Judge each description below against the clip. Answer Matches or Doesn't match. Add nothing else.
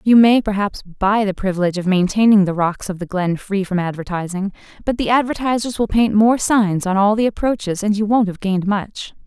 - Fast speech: Matches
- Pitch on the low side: Doesn't match